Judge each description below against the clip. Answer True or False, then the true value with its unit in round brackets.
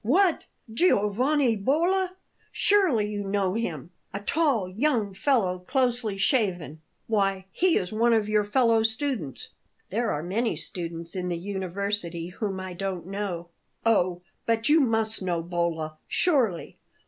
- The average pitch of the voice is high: True (205 Hz)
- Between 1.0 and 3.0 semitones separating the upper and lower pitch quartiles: False (4.7 semitones)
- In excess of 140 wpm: False (135 wpm)